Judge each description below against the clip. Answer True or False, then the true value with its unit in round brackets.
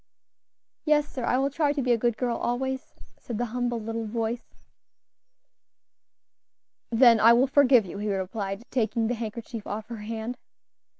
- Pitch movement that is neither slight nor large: False (2.3 semitones)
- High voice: True (235 Hz)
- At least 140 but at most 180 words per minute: True (160 wpm)